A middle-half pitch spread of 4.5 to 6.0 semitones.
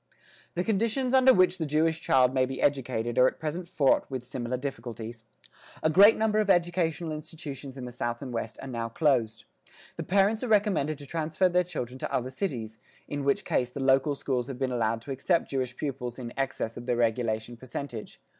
Yes: wide, 5.4 semitones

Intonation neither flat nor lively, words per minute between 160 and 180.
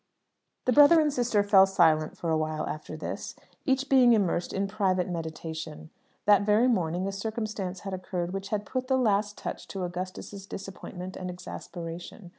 Yes: average, 3.5 semitones; average, 170 wpm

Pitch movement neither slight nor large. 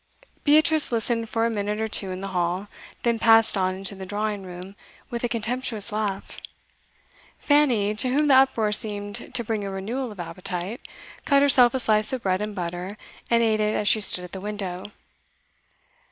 Yes: average, 3.3 semitones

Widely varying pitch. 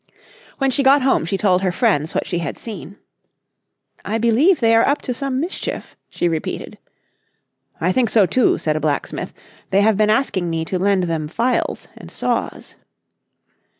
Yes: wide, 6.7 semitones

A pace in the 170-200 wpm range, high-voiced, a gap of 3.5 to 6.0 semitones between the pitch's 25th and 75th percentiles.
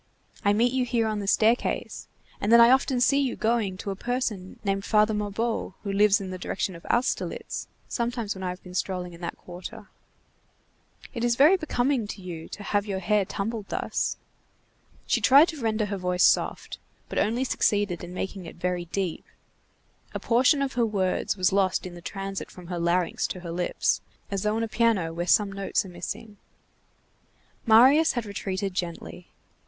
Yes: average, 190 wpm; high, 205 Hz; average, 4.1 semitones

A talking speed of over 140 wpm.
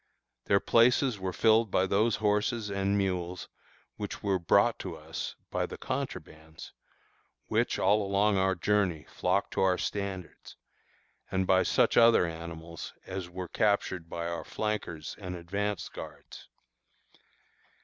No: slow, 135 wpm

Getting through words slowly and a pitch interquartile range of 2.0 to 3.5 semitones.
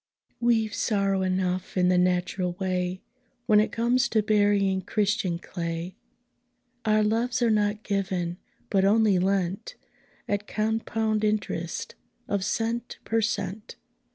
Yes: slow, 125 wpm; average, 2.8 semitones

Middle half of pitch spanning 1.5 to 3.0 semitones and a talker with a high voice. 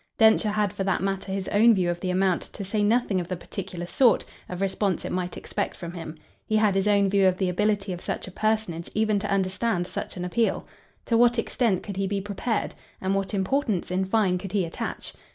Yes: narrow, 2.5 semitones; high, 195 Hz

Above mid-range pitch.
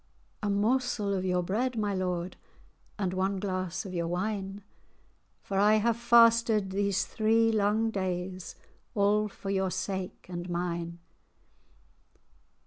Yes: high, 195 Hz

